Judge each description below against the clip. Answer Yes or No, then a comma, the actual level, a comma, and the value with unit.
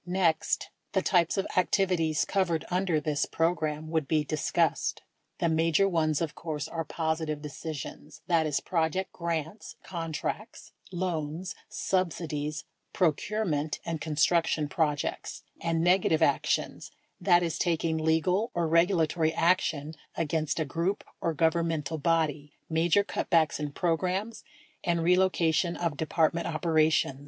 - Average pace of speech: No, slow, 125 wpm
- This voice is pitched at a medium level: Yes, medium, 165 Hz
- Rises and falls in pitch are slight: Yes, narrow, 2.0 semitones